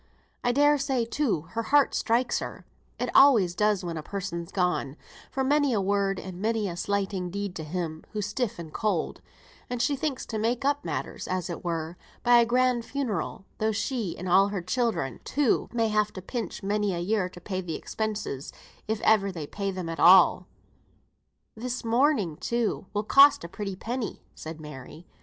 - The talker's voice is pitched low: No, high, 205 Hz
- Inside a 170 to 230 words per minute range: Yes, average, 190 wpm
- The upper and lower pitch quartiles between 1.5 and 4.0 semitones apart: No, average, 4.9 semitones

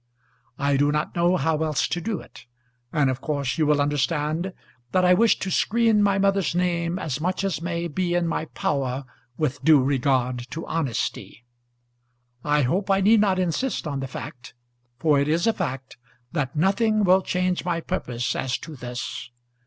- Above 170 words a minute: Yes, average, 180 wpm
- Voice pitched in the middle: Yes, medium, 160 Hz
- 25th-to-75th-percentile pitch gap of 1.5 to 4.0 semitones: No, average, 4.6 semitones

